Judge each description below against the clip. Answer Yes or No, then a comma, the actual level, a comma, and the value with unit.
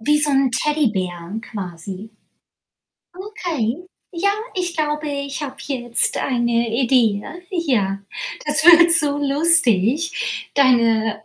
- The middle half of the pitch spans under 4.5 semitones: No, average, 5.3 semitones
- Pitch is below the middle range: No, very high, 270 Hz